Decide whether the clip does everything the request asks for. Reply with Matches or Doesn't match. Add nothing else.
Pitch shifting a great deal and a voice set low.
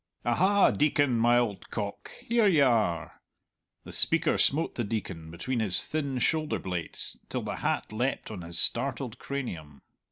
Matches